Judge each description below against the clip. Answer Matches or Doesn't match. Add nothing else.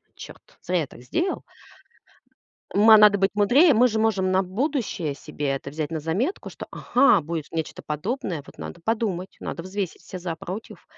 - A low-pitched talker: Doesn't match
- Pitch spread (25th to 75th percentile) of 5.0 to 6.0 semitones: Matches